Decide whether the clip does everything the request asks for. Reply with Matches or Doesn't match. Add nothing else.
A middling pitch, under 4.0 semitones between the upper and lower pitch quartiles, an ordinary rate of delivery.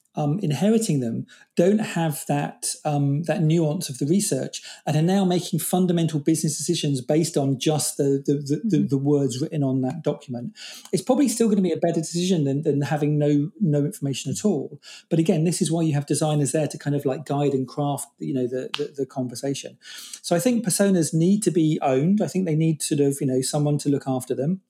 Doesn't match